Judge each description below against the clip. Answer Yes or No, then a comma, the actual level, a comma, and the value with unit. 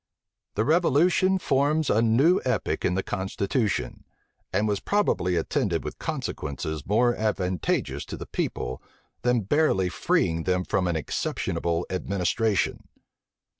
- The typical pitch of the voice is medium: No, low, 105 Hz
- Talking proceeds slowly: Yes, slow, 125 wpm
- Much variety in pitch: Yes, wide, 6.7 semitones